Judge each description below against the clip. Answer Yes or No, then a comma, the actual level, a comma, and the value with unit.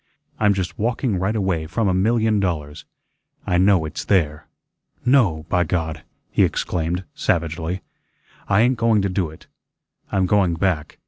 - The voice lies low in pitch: Yes, very low, 95 Hz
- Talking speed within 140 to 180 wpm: Yes, average, 150 wpm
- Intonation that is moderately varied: Yes, average, 4.1 semitones